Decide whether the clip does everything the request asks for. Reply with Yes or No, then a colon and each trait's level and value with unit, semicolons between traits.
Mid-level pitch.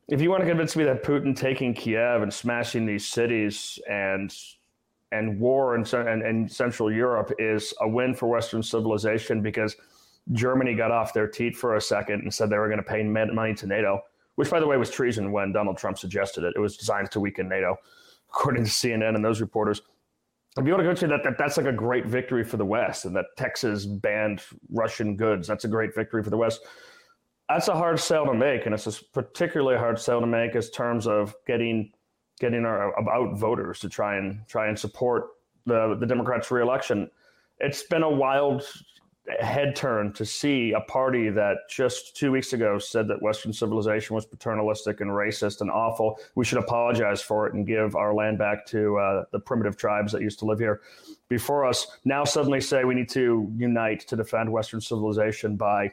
No: low, 110 Hz